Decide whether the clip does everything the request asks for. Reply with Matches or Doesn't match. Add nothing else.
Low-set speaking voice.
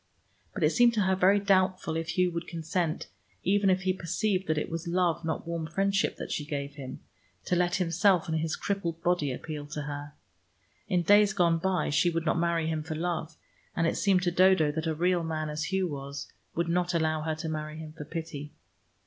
Doesn't match